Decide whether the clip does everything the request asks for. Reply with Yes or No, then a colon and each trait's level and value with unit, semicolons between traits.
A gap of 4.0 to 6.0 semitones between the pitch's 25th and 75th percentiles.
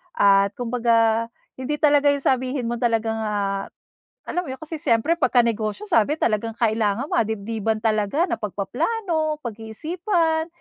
Yes: wide, 5.6 semitones